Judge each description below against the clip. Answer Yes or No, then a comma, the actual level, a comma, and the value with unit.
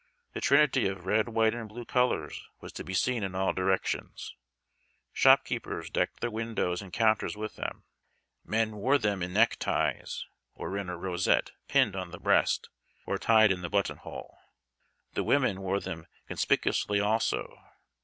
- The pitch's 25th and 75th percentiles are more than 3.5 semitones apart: No, average, 3.2 semitones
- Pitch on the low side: Yes, low, 105 Hz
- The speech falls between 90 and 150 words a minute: No, average, 165 wpm